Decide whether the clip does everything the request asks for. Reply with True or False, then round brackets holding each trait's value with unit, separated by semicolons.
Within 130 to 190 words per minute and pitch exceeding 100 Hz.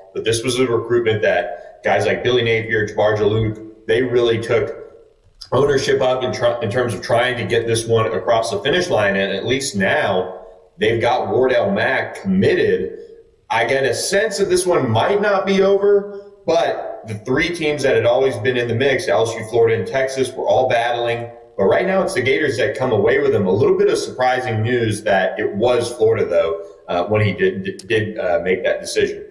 False (205 wpm; 130 Hz)